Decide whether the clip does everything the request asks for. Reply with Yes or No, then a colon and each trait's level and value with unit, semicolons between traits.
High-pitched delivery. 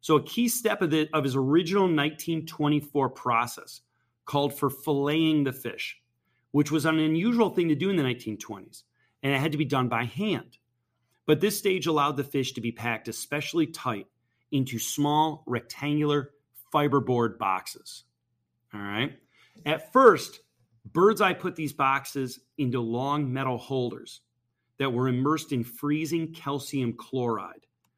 No: medium, 140 Hz